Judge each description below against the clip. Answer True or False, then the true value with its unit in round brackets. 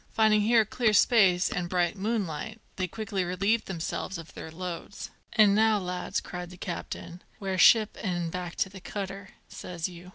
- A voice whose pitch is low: False (190 Hz)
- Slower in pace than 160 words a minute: False (175 wpm)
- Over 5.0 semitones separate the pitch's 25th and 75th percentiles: False (3.1 semitones)